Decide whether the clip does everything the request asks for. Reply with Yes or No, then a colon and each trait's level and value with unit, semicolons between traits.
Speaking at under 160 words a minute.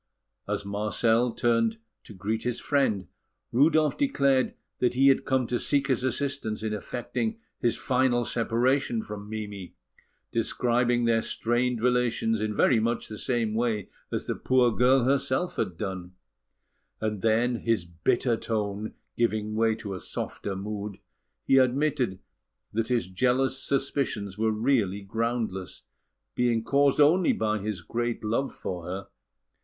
Yes: average, 140 wpm